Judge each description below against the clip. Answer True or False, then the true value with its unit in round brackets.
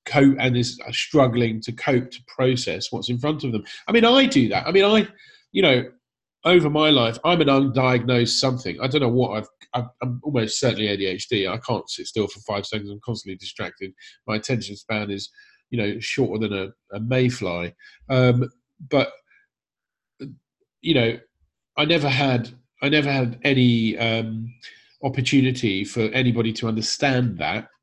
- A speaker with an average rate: True (170 wpm)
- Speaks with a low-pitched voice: True (125 Hz)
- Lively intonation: False (4.0 semitones)